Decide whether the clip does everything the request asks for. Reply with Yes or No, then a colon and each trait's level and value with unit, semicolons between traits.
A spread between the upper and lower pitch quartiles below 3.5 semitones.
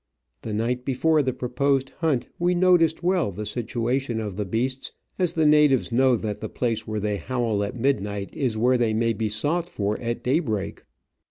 No: average, 4.4 semitones